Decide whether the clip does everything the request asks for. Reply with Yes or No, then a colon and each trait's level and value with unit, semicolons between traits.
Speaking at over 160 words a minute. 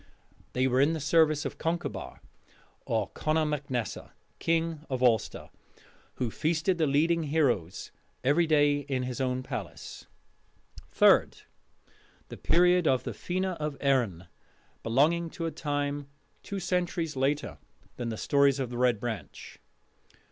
No: average, 140 wpm